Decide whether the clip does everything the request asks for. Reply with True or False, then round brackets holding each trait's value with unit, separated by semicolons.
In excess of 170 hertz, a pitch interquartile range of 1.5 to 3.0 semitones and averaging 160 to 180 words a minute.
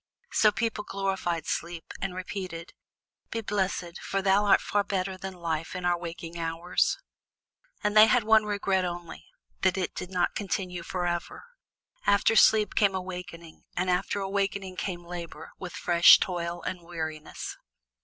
False (185 Hz; 2.4 semitones; 150 wpm)